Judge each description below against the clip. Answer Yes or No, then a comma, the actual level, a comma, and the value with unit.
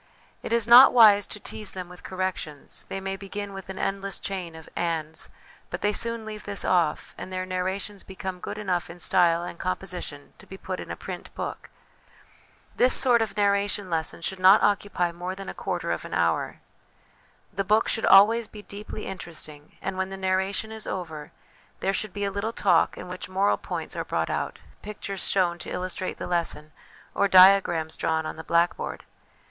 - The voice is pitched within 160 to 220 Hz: Yes, high, 190 Hz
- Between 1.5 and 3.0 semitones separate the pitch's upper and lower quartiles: Yes, narrow, 2.4 semitones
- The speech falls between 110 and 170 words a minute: No, average, 195 wpm